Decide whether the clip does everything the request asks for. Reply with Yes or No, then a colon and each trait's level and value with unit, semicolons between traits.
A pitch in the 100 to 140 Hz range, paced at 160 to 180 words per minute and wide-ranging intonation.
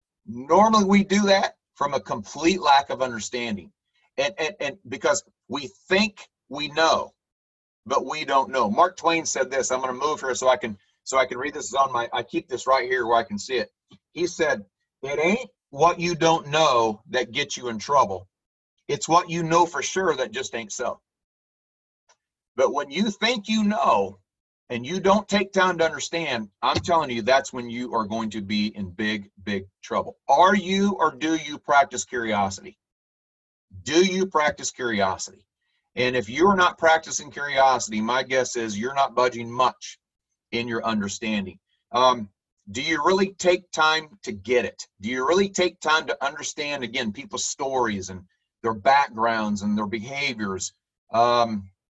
Yes: low, 135 Hz; average, 175 wpm; wide, 8.0 semitones